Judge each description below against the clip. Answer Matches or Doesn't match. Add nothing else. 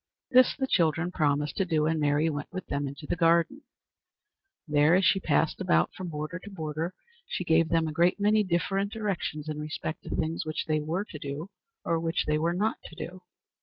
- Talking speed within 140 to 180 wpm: Doesn't match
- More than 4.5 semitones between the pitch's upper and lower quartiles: Doesn't match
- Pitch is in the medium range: Matches